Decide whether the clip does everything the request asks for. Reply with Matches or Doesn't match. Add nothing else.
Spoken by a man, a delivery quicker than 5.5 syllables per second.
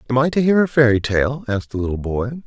Matches